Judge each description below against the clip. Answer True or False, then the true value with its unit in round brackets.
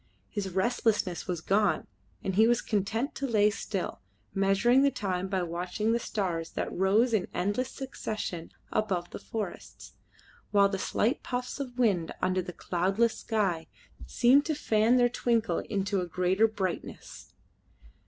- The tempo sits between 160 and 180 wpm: False (150 wpm)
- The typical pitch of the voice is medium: False (205 Hz)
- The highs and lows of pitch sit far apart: False (3.9 semitones)